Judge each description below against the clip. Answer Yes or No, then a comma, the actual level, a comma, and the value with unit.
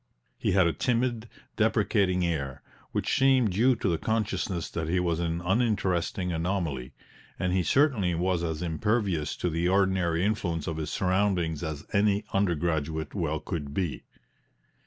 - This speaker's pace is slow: No, average, 150 wpm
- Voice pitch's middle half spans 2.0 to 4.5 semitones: Yes, average, 3.7 semitones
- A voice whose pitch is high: No, very low, 90 Hz